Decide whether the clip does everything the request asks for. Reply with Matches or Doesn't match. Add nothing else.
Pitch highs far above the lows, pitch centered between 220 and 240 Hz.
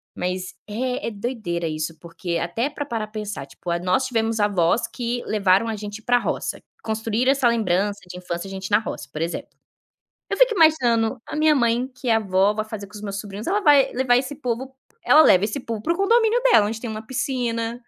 Doesn't match